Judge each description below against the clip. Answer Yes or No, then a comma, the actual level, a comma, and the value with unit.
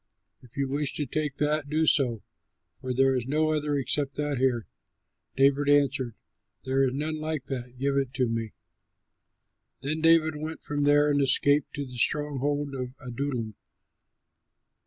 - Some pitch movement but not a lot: No, narrow, 2.3 semitones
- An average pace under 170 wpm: Yes, average, 155 wpm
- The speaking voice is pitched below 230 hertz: Yes, medium, 140 Hz